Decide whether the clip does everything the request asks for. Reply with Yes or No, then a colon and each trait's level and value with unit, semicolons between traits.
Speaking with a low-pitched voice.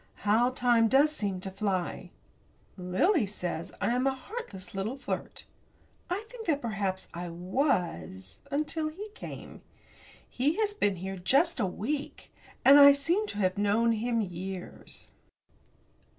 No: high, 230 Hz